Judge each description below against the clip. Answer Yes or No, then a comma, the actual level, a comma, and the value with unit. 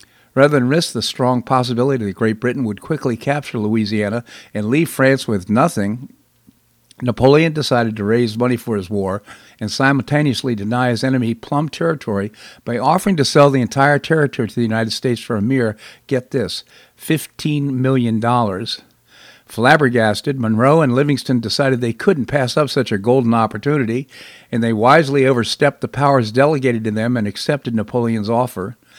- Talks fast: No, average, 160 wpm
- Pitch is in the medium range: No, low, 125 Hz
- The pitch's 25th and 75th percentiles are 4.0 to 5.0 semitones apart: No, average, 3.5 semitones